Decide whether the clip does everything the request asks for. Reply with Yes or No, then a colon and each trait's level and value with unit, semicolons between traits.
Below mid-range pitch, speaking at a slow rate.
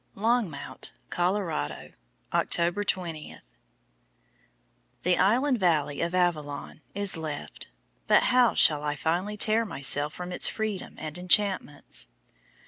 No: medium, 180 Hz; slow, 110 wpm